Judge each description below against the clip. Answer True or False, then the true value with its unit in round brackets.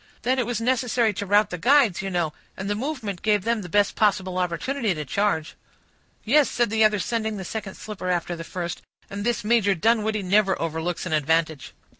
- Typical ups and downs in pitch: True (4.1 semitones)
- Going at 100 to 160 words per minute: False (200 wpm)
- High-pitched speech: True (205 Hz)